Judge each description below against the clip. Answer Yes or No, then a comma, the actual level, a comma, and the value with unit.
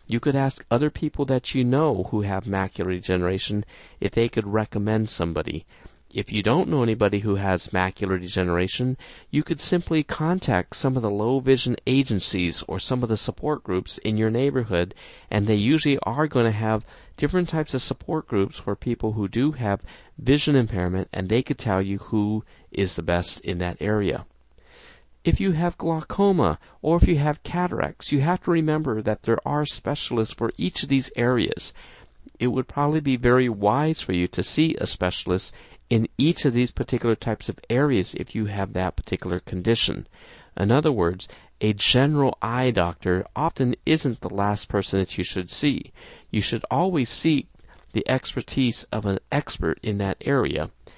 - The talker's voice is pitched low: Yes, low, 110 Hz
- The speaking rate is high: No, average, 180 wpm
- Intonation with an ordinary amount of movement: No, wide, 6.0 semitones